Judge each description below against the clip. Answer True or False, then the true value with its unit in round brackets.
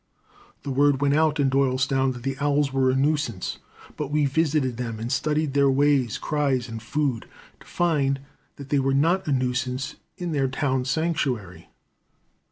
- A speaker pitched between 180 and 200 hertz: False (135 Hz)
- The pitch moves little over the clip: True (2.2 semitones)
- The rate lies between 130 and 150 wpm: False (170 wpm)